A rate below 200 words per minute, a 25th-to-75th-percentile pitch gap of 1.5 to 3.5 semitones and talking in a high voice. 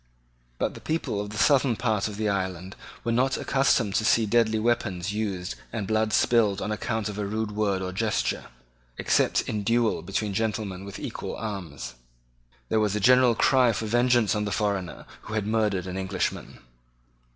No: average, 180 wpm; narrow, 2.4 semitones; low, 105 Hz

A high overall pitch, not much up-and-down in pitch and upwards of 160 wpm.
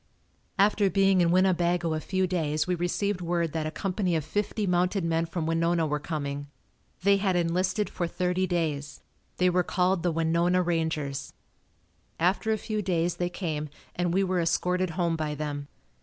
No: medium, 175 Hz; narrow, 2.3 semitones; average, 170 wpm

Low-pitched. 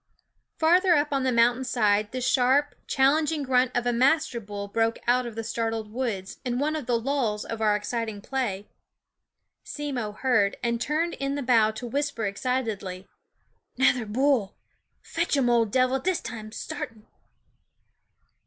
No: high, 245 Hz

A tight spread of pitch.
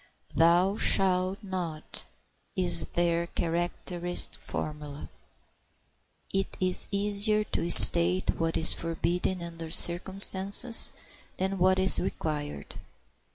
Yes: narrow, 2.3 semitones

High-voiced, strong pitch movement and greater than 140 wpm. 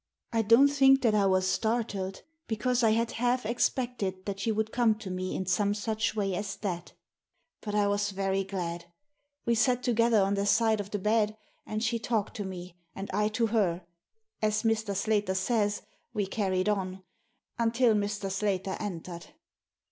No: high, 210 Hz; average, 2.8 semitones; average, 180 wpm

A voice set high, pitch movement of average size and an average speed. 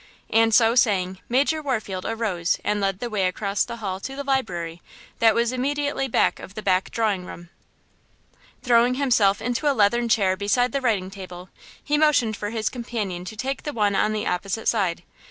Yes: high, 220 Hz; average, 4.3 semitones; average, 190 wpm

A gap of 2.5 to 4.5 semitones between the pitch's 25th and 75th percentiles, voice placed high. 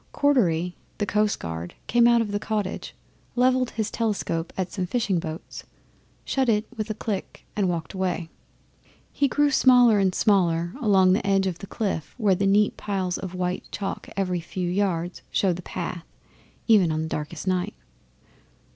Yes: average, 3.4 semitones; high, 195 Hz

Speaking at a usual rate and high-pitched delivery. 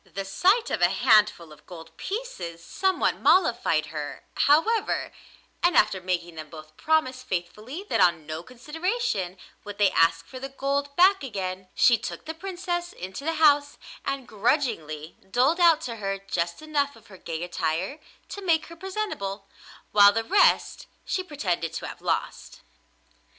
Yes: average, 160 wpm; high, 225 Hz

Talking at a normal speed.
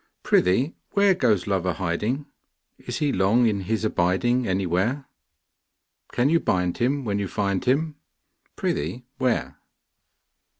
No: slow, 130 wpm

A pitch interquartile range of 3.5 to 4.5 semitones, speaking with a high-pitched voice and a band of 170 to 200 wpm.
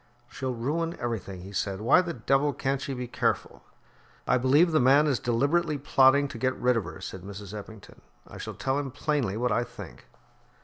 No: average, 3.8 semitones; low, 130 Hz; average, 195 wpm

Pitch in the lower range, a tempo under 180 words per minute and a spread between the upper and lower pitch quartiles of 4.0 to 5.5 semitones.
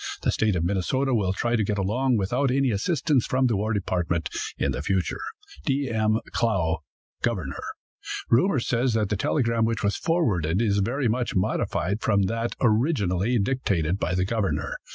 Yes: low, 110 Hz; average, 170 wpm; average, 4.5 semitones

